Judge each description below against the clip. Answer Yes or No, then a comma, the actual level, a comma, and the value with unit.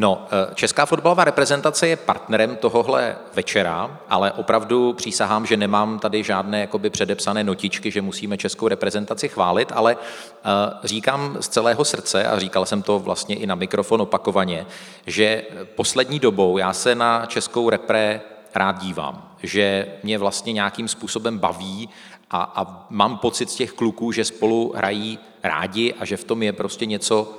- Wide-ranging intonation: No, narrow, 2.4 semitones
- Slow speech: No, average, 155 wpm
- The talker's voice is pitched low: Yes, low, 110 Hz